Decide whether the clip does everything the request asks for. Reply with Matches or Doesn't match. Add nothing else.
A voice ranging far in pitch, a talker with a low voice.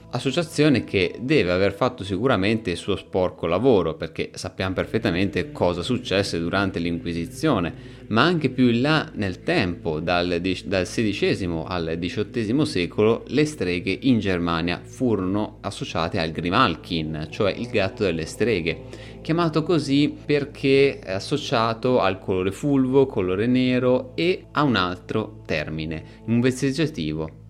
Matches